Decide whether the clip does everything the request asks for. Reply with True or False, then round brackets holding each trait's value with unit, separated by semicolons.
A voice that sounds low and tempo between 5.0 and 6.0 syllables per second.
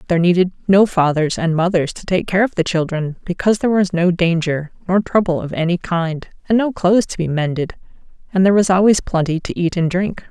False (180 Hz; 5.9 syllables/s)